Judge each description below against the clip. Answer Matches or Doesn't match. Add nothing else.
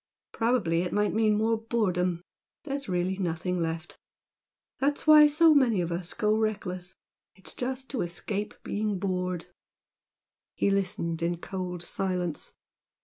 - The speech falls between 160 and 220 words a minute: Doesn't match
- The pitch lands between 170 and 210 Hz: Matches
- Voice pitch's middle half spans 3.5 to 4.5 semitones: Matches